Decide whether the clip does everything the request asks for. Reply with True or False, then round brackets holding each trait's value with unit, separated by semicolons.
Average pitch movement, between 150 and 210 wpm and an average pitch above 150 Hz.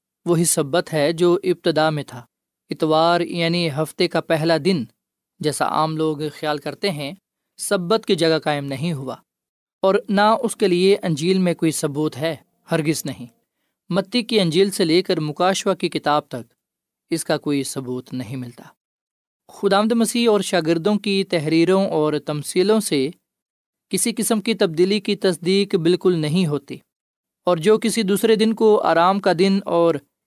True (4.2 semitones; 160 wpm; 175 Hz)